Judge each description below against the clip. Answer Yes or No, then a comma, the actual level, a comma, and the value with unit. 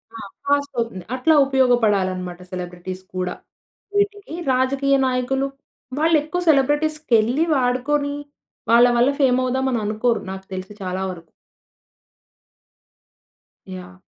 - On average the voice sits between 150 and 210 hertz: No, very high, 250 Hz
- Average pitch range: No, wide, 6.7 semitones